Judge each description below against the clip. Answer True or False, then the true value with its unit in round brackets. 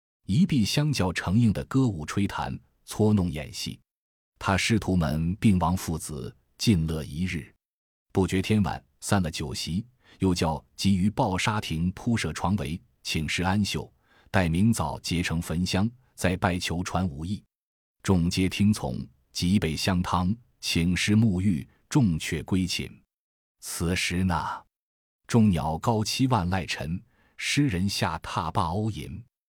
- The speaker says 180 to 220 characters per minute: True (195 characters per minute)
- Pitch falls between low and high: False (95 Hz)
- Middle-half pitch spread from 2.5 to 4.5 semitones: True (3.9 semitones)